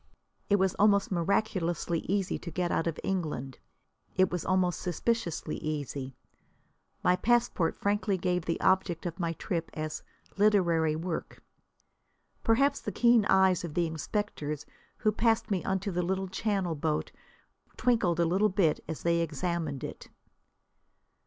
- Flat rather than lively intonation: No, average, 3.4 semitones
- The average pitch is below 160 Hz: No, medium, 180 Hz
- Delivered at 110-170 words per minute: Yes, average, 140 wpm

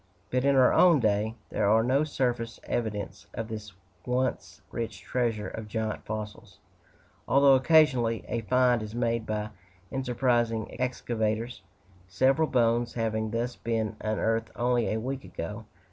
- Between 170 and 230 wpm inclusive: No, average, 140 wpm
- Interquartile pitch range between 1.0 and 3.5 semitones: Yes, narrow, 2.5 semitones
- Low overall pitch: Yes, low, 115 Hz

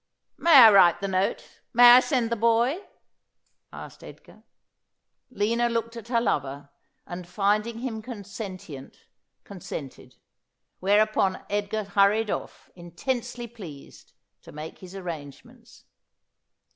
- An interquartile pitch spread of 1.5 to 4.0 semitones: No, average, 4.4 semitones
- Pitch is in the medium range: No, high, 205 Hz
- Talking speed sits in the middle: No, slow, 125 wpm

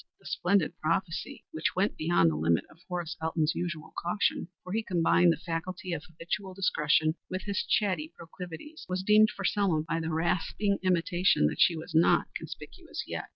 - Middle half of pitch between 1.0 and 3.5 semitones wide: Yes, average, 2.7 semitones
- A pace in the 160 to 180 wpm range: Yes, average, 175 wpm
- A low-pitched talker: No, medium, 175 Hz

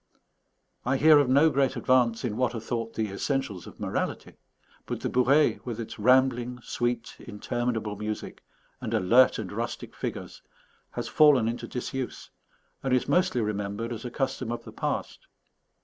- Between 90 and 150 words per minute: No, average, 160 wpm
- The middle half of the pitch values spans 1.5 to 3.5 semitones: Yes, average, 2.8 semitones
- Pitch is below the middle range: Yes, low, 120 Hz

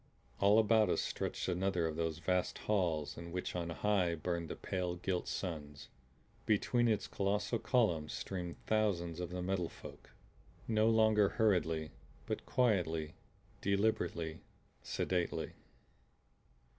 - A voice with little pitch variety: No, average, 3.8 semitones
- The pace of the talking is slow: Yes, slow, 125 wpm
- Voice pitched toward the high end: No, very low, 90 Hz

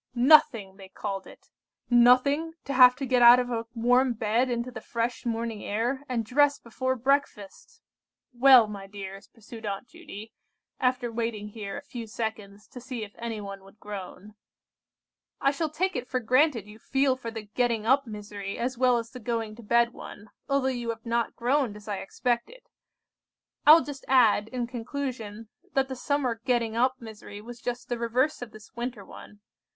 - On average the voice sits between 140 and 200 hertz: No, high, 235 Hz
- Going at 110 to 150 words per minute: No, average, 180 wpm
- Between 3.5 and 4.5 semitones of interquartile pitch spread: No, average, 3.1 semitones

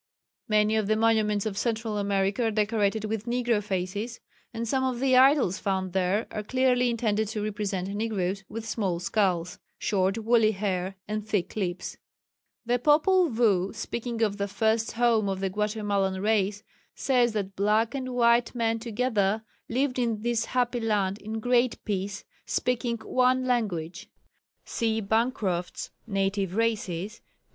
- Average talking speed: Yes, average, 150 wpm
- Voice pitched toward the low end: No, high, 215 Hz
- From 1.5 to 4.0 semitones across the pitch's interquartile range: Yes, average, 3.1 semitones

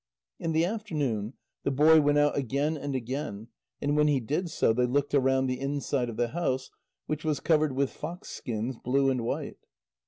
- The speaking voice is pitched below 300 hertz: Yes, medium, 140 Hz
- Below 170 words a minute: No, average, 190 wpm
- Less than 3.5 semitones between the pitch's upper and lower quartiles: Yes, average, 2.9 semitones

